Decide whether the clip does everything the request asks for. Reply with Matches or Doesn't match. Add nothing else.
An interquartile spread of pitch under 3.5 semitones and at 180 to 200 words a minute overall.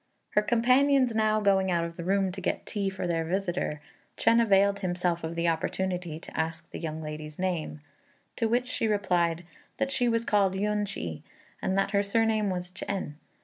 Doesn't match